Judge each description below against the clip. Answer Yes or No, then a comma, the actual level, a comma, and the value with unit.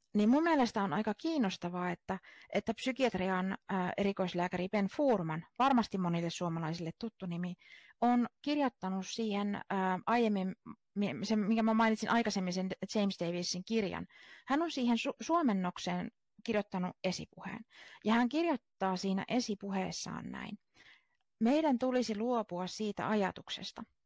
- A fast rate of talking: No, average, 125 wpm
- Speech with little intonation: No, average, 4.0 semitones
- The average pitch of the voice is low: No, high, 210 Hz